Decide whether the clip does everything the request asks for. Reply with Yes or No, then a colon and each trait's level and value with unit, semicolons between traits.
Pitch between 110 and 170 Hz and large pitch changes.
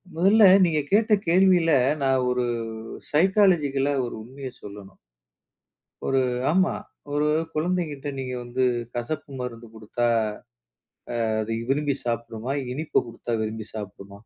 Yes: low, 135 Hz; wide, 5.7 semitones